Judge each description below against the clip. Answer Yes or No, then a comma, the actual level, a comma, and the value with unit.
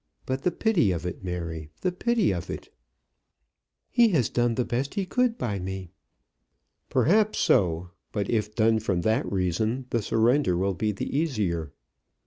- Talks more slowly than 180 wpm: Yes, average, 160 wpm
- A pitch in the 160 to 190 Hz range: No, low, 110 Hz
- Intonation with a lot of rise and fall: Yes, wide, 7.7 semitones